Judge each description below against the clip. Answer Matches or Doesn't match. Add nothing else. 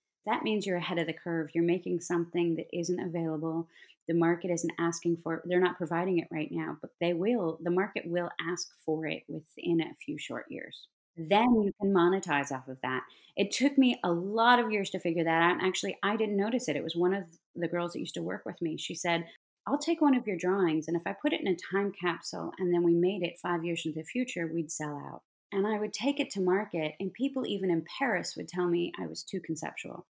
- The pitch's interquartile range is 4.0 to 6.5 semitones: Doesn't match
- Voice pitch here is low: Doesn't match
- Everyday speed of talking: Doesn't match